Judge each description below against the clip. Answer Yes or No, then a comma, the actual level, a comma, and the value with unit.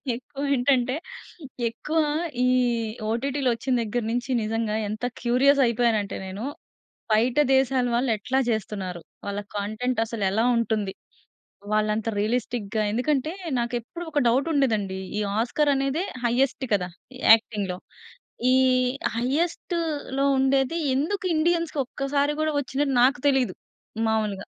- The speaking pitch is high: Yes, high, 245 Hz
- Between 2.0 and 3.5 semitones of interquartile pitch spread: No, average, 4.0 semitones